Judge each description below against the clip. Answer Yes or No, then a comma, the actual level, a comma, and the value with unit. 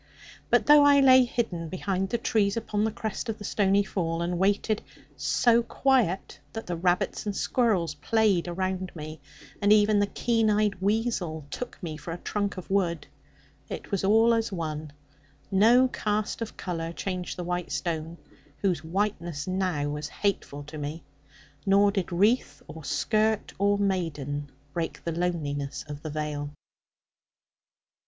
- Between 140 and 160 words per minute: Yes, average, 155 wpm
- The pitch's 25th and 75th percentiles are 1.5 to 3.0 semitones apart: No, average, 4.4 semitones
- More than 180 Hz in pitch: Yes, high, 190 Hz